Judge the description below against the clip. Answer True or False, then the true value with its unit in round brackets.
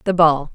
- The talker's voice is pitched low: False (165 Hz)